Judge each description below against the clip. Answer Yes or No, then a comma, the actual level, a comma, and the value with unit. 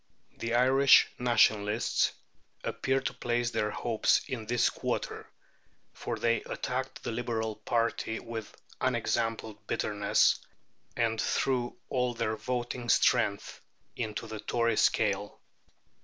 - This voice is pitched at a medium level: No, low, 115 Hz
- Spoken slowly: Yes, slow, 110 wpm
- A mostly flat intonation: Yes, narrow, 1.9 semitones